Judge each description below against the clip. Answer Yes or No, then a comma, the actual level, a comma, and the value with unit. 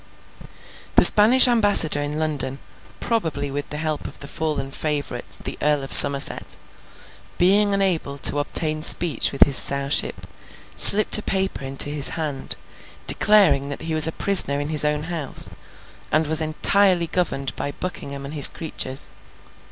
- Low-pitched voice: No, medium, 155 Hz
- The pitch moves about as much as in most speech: Yes, average, 3.9 semitones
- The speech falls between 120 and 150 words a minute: Yes, average, 145 wpm